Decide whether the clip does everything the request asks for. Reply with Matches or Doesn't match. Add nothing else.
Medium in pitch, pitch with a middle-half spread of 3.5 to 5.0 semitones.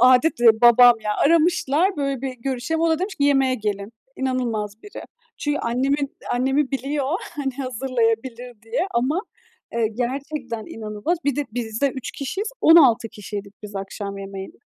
Doesn't match